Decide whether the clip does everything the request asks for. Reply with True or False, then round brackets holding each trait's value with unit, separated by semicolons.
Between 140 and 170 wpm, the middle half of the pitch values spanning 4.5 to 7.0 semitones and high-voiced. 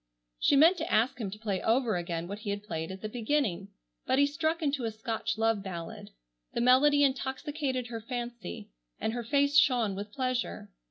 False (185 wpm; 4.9 semitones; 235 Hz)